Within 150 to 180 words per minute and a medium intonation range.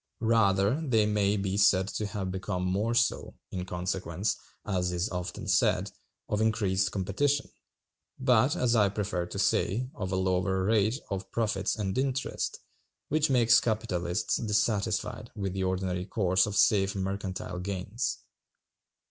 No: average, 140 wpm; average, 3.0 semitones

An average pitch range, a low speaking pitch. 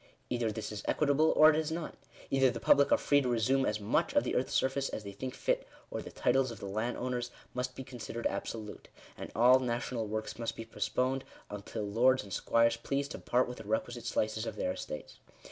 Yes: average, 3.3 semitones; low, 120 Hz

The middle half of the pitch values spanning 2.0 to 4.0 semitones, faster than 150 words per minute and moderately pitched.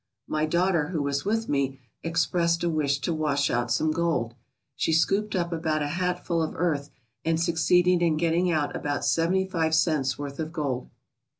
Yes: average, 2.9 semitones; average, 180 wpm; medium, 160 Hz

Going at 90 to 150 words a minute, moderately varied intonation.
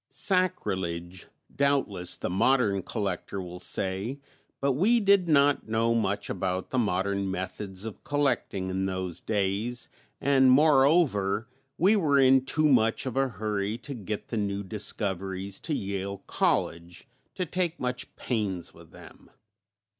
No: average, 140 wpm; wide, 6.1 semitones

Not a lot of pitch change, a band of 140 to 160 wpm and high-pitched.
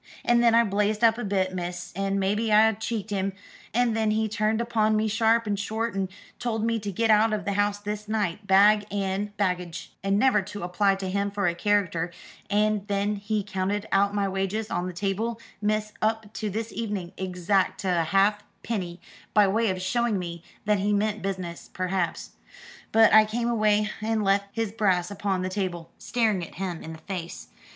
No: narrow, 2.2 semitones; average, 195 wpm; high, 205 Hz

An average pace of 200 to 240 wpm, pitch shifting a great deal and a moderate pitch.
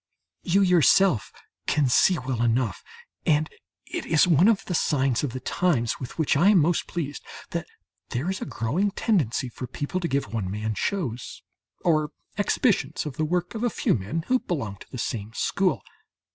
No: average, 185 wpm; wide, 6.6 semitones; medium, 150 Hz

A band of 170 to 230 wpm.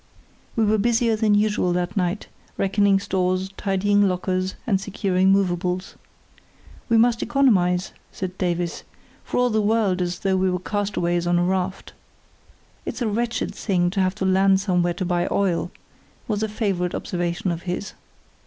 No: average, 160 wpm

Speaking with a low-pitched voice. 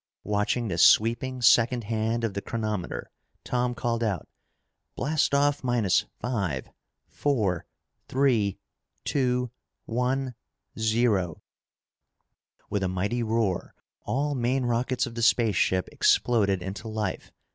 Yes: low, 115 Hz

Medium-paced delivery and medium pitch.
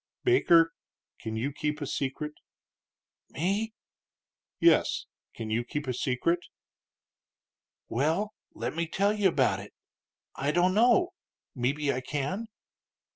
No: slow, 120 wpm; medium, 150 Hz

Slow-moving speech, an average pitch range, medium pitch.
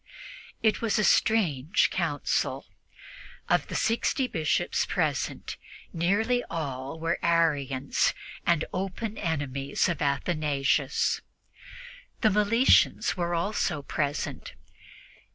No: slow, 95 wpm; wide, 6.4 semitones; medium, 170 Hz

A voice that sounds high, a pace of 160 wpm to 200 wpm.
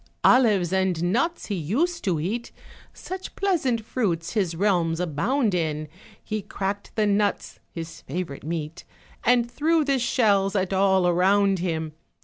No: high, 195 Hz; average, 140 wpm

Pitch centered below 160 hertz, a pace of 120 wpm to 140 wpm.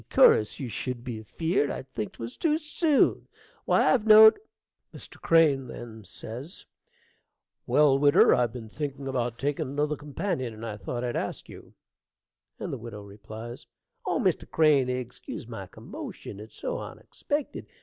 Yes: low, 135 Hz; slow, 135 wpm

